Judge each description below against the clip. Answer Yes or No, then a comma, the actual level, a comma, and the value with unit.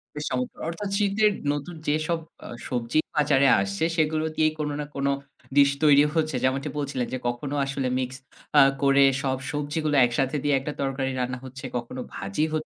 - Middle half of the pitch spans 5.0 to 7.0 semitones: No, average, 2.7 semitones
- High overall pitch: No, medium, 140 Hz